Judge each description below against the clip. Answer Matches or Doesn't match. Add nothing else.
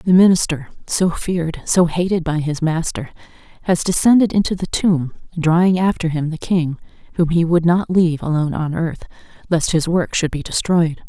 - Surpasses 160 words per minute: Matches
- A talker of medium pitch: Matches